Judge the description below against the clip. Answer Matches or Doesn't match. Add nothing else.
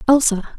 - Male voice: Doesn't match